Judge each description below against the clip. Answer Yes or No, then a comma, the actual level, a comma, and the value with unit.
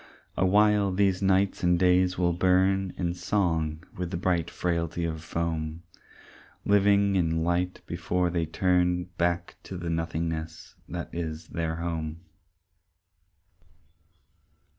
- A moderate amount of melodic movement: No, narrow, 1.9 semitones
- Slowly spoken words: Yes, slow, 120 wpm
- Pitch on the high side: No, very low, 85 Hz